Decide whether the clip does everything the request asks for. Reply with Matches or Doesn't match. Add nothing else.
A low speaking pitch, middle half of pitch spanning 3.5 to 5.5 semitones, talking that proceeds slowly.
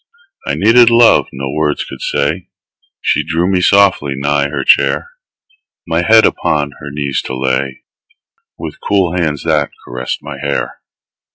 Doesn't match